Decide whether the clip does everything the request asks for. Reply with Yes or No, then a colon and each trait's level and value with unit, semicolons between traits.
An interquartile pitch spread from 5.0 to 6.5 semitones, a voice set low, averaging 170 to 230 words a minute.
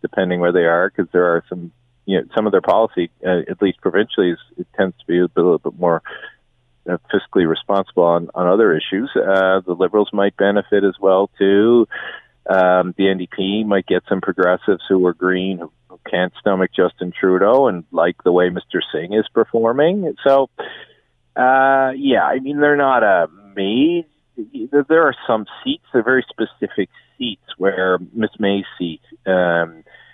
Yes: average, 5.3 semitones; low, 100 Hz; average, 175 wpm